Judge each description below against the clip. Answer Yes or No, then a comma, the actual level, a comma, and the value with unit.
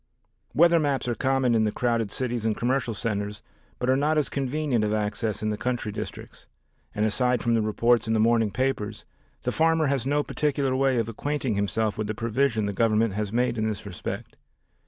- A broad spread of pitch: No, average, 3.7 semitones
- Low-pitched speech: Yes, low, 115 Hz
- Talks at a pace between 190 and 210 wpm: Yes, average, 200 wpm